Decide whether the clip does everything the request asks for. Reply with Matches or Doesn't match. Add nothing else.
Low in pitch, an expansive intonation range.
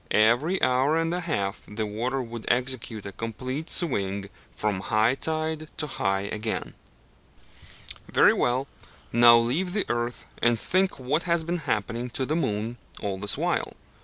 Matches